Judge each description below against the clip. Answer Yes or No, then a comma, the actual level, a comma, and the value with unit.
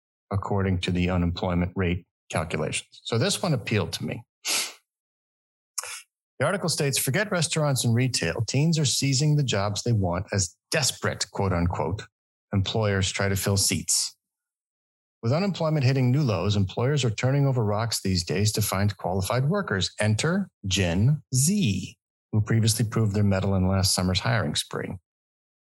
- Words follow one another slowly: No, average, 150 wpm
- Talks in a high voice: No, low, 105 Hz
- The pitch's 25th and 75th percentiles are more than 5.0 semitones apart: Yes, wide, 5.5 semitones